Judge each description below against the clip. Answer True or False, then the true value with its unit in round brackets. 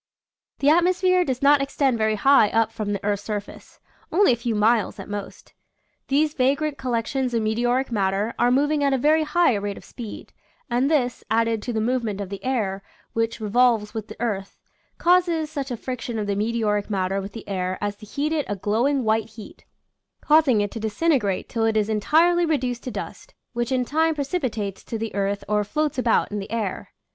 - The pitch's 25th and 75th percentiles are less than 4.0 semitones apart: False (5.0 semitones)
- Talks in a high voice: True (235 Hz)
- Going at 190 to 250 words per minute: True (205 wpm)